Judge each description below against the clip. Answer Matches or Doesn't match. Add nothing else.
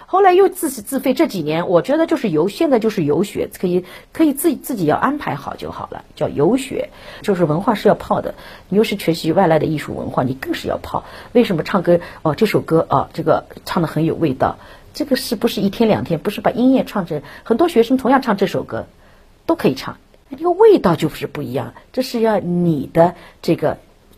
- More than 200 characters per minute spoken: Matches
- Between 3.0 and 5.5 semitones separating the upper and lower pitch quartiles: Doesn't match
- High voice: Matches